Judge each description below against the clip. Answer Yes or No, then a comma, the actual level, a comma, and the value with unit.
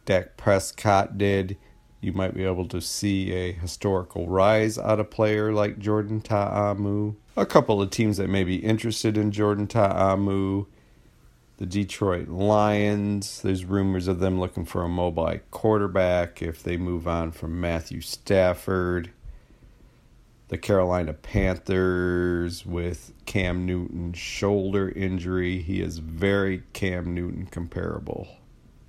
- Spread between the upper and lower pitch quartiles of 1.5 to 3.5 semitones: Yes, narrow, 2.4 semitones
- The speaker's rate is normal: No, slow, 130 wpm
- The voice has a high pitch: No, very low, 95 Hz